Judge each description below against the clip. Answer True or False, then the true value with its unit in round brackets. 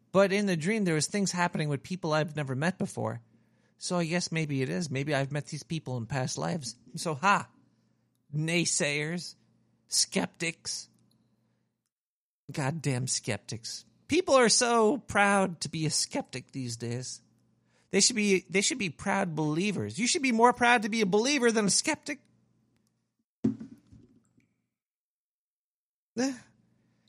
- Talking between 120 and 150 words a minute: True (140 wpm)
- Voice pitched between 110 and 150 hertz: False (165 Hz)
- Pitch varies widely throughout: True (7.4 semitones)